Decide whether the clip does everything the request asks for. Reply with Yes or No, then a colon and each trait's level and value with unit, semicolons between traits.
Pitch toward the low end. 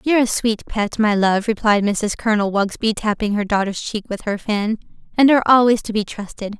No: high, 215 Hz